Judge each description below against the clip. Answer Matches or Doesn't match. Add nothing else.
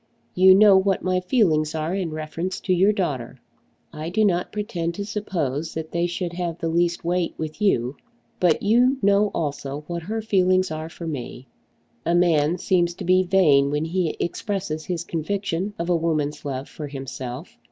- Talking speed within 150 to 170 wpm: Doesn't match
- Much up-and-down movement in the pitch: Doesn't match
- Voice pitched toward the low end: Doesn't match